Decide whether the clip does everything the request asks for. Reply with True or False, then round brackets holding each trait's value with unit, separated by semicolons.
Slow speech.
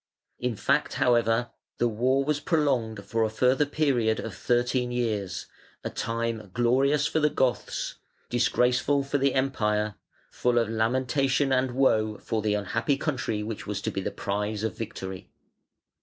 False (155 wpm)